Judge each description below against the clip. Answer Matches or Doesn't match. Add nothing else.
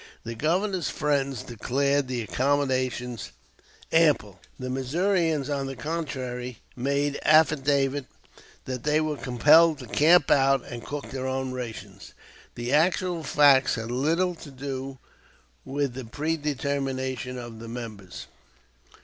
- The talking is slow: Matches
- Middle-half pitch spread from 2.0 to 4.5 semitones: Matches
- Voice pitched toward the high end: Doesn't match